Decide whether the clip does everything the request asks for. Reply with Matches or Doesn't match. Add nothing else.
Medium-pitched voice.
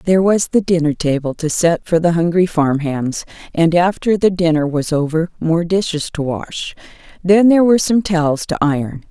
Matches